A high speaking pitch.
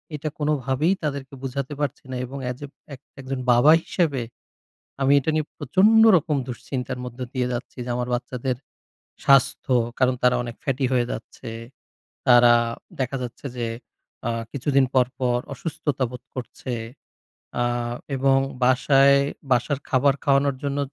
No: low, 135 Hz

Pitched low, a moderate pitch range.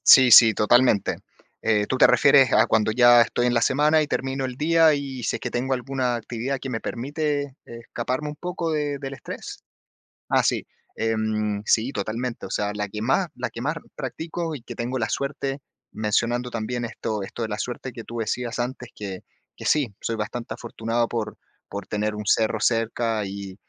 Yes: low, 120 Hz; average, 3.5 semitones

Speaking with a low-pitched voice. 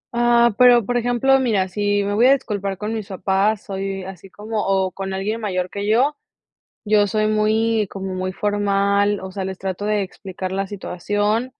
No: high, 205 Hz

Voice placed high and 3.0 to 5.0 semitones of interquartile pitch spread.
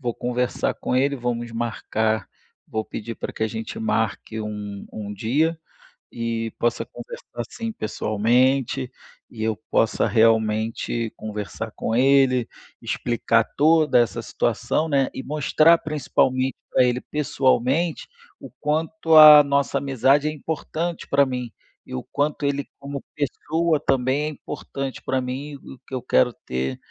No: low, 130 Hz; average, 4.4 semitones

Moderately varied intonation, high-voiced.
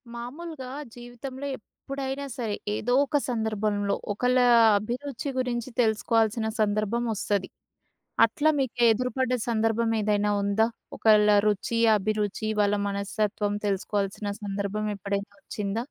Yes: average, 3.1 semitones; high, 220 Hz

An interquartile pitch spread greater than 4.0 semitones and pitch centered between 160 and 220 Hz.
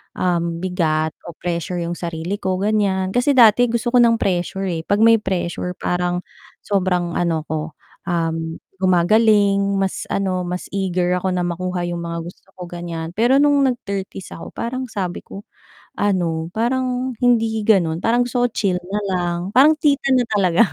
Yes: average, 4.4 semitones; high, 190 Hz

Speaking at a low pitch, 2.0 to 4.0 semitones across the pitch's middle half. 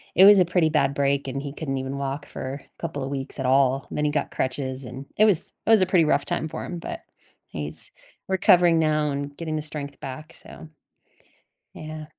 No: medium, 145 Hz; average, 2.7 semitones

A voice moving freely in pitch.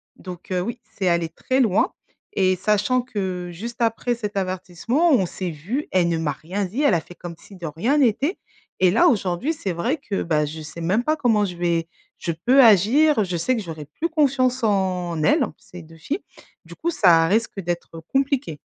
Yes: wide, 6.3 semitones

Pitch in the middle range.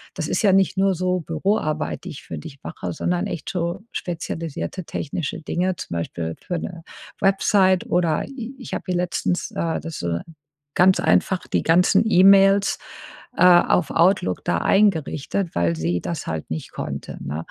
Yes: medium, 170 Hz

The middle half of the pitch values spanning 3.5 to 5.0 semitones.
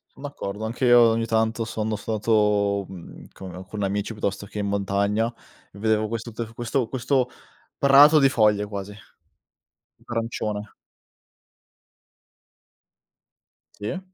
No: narrow, 2.4 semitones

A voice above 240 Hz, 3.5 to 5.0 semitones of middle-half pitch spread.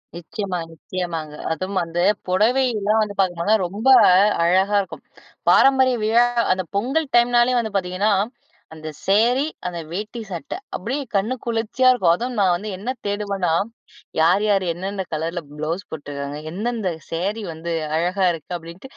No: high, 195 Hz; average, 4.5 semitones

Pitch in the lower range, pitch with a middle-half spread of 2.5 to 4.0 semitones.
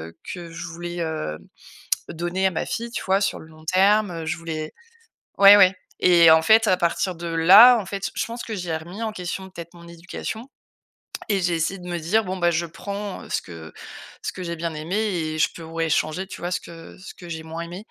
No: medium, 175 Hz; average, 2.9 semitones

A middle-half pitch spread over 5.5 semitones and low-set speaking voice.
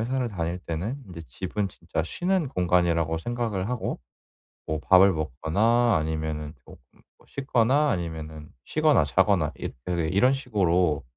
Yes: wide, 7.0 semitones; very low, 90 Hz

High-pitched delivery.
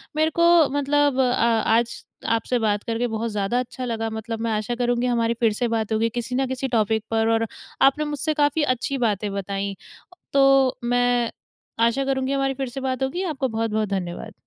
Yes: high, 240 Hz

